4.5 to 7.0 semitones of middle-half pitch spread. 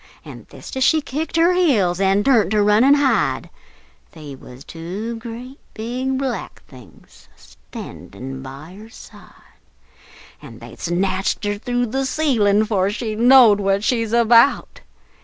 Yes: average, 5.1 semitones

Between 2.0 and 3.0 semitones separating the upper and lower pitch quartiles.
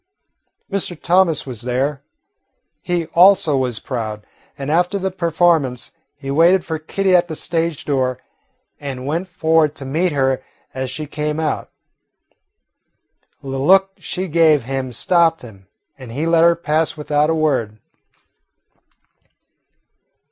No: average, 4.3 semitones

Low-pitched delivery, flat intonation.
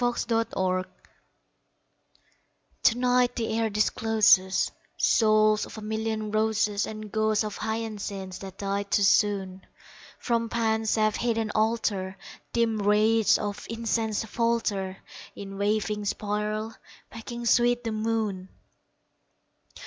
No: high, 215 Hz; narrow, 1.9 semitones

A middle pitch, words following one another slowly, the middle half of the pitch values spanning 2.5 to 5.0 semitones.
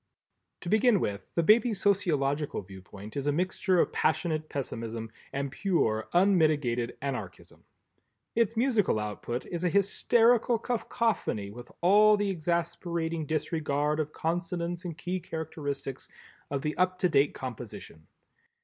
No: medium, 160 Hz; slow, 130 wpm; wide, 5.4 semitones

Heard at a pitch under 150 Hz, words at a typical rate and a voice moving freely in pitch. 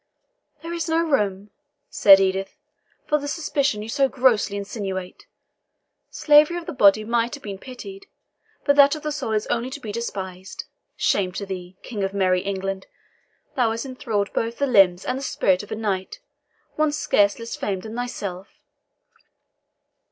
No: high, 220 Hz; average, 165 wpm; wide, 6.1 semitones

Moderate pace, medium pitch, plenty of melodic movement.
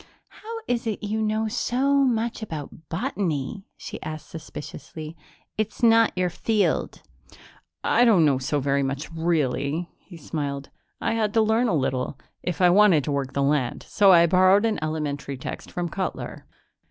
Yes: average, 165 wpm; medium, 175 Hz; wide, 6.8 semitones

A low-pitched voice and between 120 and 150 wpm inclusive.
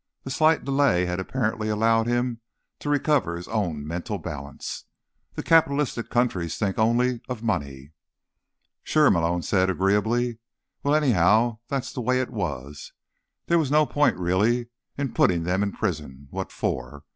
Yes: low, 110 Hz; average, 145 wpm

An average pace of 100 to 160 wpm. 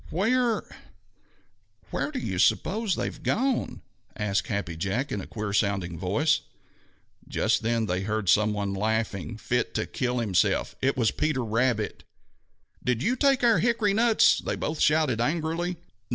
Yes: average, 150 wpm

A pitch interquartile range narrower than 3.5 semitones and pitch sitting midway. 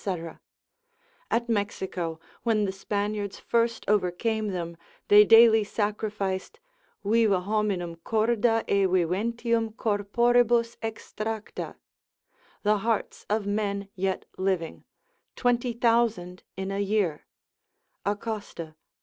No: average, 2.8 semitones; high, 210 Hz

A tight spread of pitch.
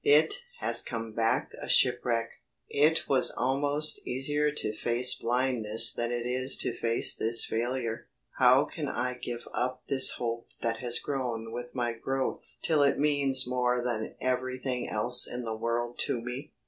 Yes: narrow, 2.1 semitones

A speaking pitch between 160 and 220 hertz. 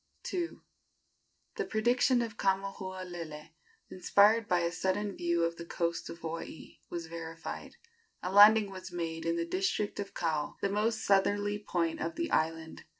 Yes: medium, 185 Hz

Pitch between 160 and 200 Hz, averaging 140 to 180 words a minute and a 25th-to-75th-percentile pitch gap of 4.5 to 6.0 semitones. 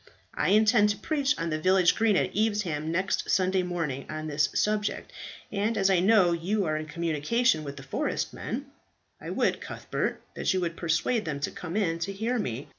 No: medium, 185 Hz; average, 195 wpm; average, 5.1 semitones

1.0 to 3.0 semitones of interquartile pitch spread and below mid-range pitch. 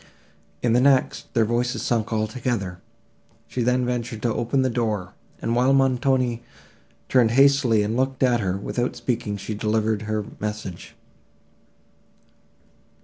Yes: average, 2.7 semitones; low, 120 Hz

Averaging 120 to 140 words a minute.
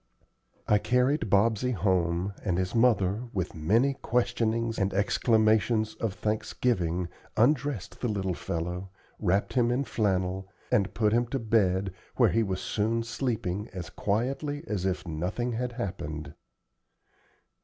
Yes: slow, 135 wpm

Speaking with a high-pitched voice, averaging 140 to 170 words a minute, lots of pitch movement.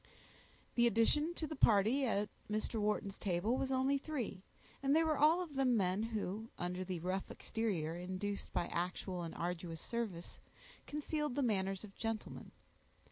Yes: high, 215 Hz; average, 160 wpm; wide, 6.2 semitones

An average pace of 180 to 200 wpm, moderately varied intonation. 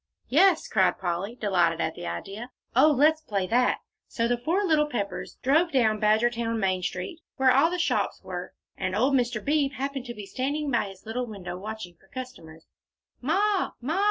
No: average, 185 wpm; wide, 6.3 semitones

